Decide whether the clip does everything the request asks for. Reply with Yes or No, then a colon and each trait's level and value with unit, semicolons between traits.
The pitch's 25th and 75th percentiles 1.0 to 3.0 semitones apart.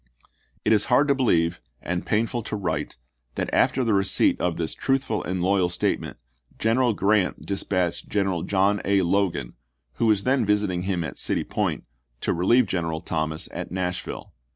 No: average, 3.7 semitones